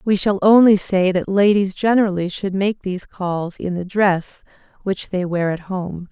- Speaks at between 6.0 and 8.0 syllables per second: No, 4.5 syllables/s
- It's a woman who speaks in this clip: Yes, female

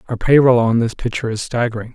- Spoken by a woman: No, male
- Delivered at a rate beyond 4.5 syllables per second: Yes, 6.8 syllables/s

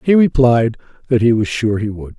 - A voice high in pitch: No, low, 120 Hz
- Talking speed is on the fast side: Yes, fast, 220 wpm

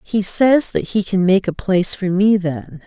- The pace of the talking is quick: Yes, fast, 230 wpm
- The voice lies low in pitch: No, high, 190 Hz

